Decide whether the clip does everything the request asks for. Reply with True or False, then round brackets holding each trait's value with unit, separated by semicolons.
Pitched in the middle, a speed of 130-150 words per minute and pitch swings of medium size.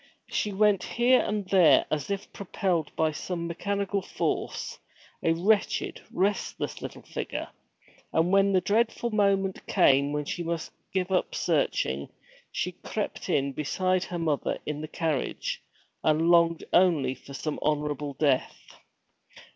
True (170 Hz; 140 wpm; 4.5 semitones)